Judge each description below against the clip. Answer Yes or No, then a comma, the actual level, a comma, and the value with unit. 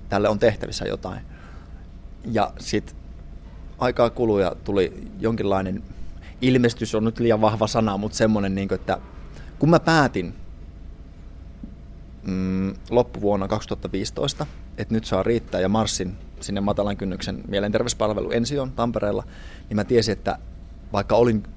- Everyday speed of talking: Yes, average, 120 wpm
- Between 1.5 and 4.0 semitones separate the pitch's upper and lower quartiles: No, average, 4.6 semitones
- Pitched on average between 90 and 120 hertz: Yes, low, 100 Hz